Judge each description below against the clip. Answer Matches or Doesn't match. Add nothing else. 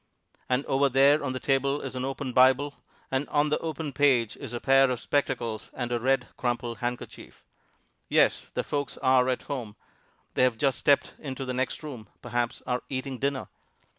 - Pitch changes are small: Matches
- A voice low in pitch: Matches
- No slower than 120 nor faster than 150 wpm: Doesn't match